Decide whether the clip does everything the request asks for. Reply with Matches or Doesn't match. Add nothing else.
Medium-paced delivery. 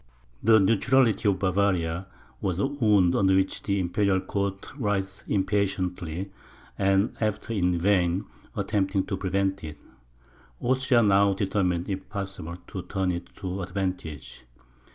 Doesn't match